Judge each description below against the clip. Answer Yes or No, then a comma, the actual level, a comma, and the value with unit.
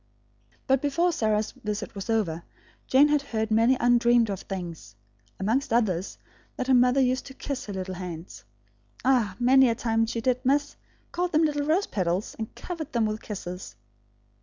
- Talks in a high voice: Yes, high, 230 Hz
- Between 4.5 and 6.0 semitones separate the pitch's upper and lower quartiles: Yes, average, 4.9 semitones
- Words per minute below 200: Yes, average, 170 wpm